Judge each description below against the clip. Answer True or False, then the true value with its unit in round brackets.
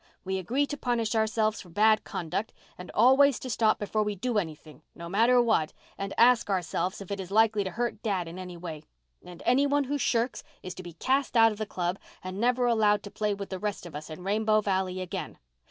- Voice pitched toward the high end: True (210 Hz)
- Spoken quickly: True (225 wpm)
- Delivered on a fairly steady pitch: False (4.0 semitones)